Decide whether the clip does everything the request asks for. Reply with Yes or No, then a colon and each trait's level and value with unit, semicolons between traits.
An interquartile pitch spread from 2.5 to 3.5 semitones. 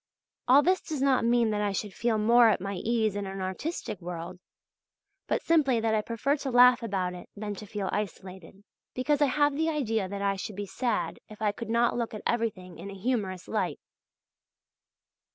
No: average, 4.0 semitones